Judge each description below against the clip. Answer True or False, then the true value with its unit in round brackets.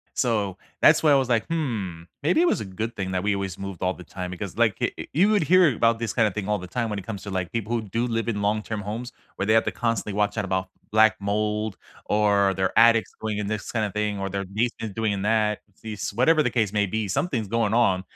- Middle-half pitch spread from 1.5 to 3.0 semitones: True (2.7 semitones)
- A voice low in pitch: True (105 Hz)